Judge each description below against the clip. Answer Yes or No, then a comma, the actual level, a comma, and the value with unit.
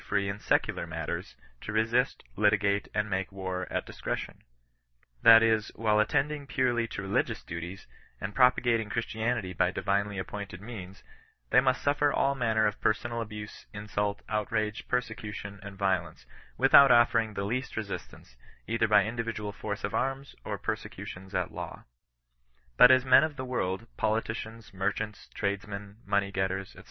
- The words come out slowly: No, average, 150 wpm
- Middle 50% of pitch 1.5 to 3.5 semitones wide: Yes, average, 2.8 semitones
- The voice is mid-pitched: No, low, 105 Hz